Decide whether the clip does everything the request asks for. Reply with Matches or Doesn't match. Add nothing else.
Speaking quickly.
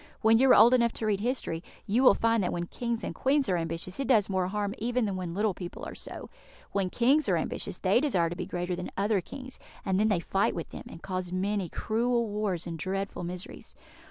Matches